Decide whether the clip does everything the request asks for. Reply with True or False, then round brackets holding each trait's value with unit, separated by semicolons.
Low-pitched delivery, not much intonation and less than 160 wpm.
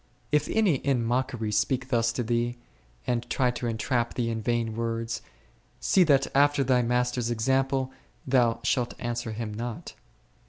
True (120 Hz; 2.2 semitones; 150 wpm)